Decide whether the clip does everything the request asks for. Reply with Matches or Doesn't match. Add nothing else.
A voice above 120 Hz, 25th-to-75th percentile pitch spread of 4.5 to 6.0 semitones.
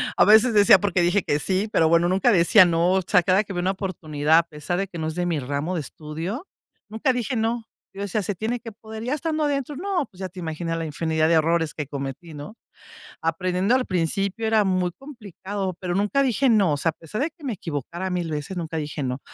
Matches